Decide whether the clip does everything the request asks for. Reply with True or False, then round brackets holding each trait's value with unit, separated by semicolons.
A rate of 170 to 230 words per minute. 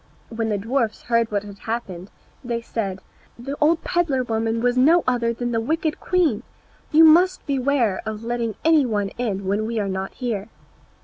True (180 wpm)